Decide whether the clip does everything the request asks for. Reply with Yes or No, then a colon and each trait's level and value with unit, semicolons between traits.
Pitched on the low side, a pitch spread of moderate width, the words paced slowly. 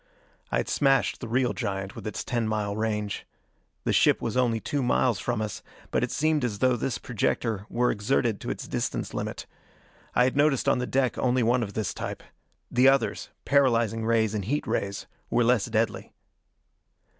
No: low, 115 Hz; average, 3.0 semitones; average, 185 wpm